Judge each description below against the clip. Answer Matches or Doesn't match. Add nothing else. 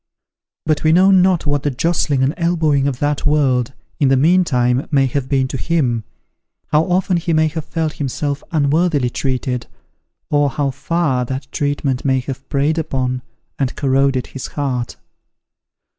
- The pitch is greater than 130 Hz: Matches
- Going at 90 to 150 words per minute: Doesn't match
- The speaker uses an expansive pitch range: Doesn't match